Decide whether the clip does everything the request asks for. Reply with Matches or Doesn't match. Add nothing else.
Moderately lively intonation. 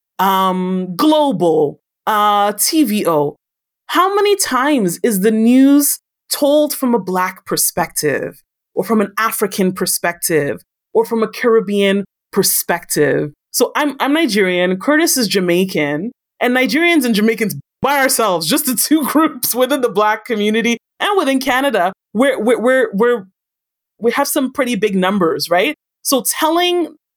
Doesn't match